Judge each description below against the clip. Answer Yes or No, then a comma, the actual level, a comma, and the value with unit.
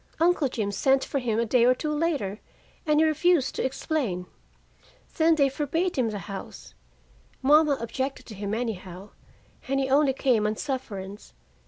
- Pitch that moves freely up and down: Yes, wide, 5.8 semitones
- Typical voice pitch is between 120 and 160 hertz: No, very high, 260 Hz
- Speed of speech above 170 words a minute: No, average, 165 wpm